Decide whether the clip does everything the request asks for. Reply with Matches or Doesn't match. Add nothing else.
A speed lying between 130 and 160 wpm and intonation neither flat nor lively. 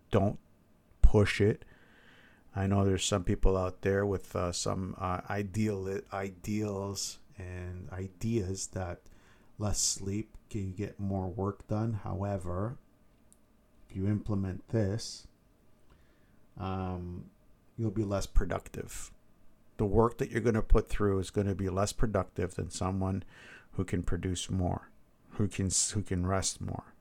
Doesn't match